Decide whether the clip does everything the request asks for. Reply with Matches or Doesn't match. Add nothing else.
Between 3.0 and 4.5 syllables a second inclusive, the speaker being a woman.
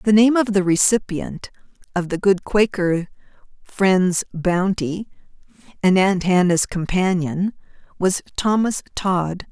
Matches